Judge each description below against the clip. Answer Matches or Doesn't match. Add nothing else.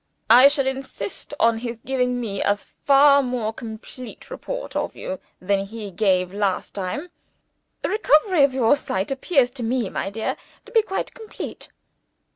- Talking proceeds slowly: Doesn't match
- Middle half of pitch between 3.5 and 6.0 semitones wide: Matches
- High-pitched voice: Matches